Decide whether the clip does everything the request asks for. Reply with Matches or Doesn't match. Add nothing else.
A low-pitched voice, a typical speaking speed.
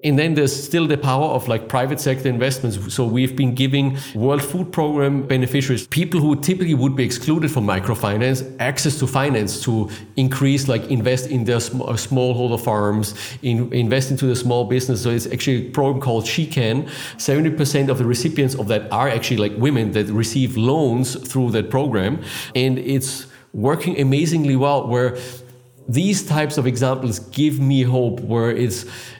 Matches